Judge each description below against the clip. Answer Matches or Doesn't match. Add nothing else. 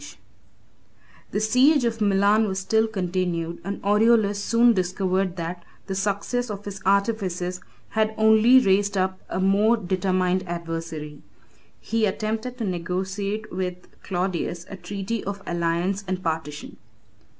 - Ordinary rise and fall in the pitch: Matches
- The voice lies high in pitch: Matches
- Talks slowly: Matches